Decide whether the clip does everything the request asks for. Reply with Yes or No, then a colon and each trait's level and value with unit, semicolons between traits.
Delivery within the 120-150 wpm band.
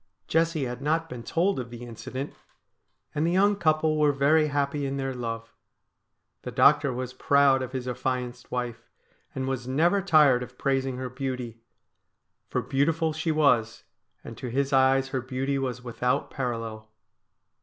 No: average, 160 wpm